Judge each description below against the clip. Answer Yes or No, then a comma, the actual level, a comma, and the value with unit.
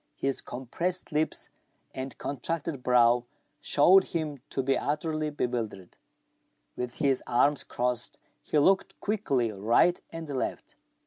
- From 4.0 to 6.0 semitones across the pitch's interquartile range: Yes, average, 4.4 semitones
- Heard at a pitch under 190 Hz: Yes, low, 135 Hz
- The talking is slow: Yes, slow, 120 wpm